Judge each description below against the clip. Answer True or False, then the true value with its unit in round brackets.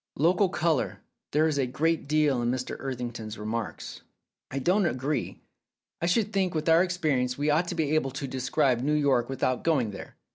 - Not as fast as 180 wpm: False (195 wpm)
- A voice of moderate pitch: True (145 Hz)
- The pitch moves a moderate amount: True (4.4 semitones)